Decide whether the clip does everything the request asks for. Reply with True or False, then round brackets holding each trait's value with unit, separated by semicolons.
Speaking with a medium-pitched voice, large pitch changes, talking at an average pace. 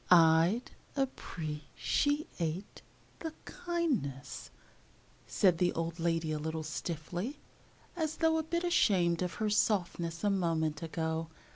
False (175 Hz; 7.6 semitones; 130 wpm)